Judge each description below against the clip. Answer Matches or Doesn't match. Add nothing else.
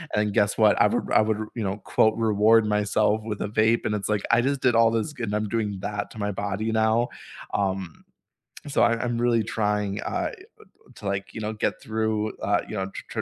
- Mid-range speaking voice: Doesn't match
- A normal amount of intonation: Doesn't match